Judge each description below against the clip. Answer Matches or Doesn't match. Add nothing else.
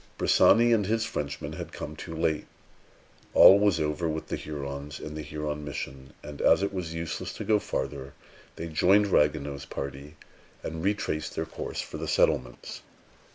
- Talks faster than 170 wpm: Doesn't match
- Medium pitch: Doesn't match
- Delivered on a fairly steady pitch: Doesn't match